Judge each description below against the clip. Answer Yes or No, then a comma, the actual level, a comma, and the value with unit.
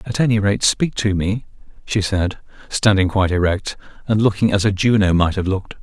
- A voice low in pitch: Yes, low, 100 Hz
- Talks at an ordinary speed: Yes, average, 195 wpm